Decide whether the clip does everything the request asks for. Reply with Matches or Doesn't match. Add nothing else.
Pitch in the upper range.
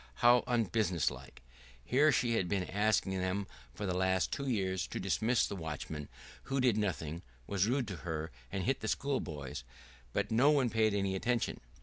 Doesn't match